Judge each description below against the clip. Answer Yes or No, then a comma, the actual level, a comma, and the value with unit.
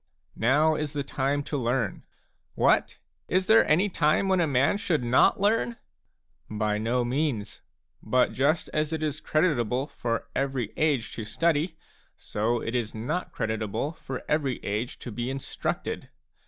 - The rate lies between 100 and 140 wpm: No, average, 160 wpm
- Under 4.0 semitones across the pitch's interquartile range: No, average, 4.9 semitones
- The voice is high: No, low, 135 Hz